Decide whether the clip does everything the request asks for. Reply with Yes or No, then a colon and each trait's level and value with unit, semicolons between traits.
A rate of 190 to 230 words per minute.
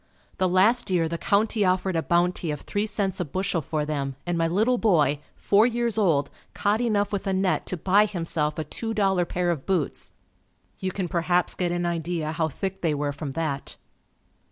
Yes: average, 200 wpm